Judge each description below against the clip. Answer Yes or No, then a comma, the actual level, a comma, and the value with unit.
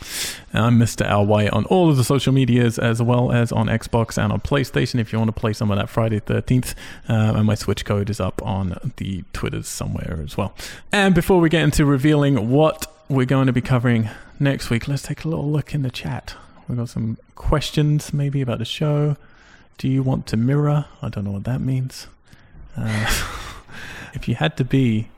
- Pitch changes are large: No, average, 4.7 semitones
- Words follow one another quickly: Yes, fast, 210 wpm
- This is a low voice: Yes, low, 120 Hz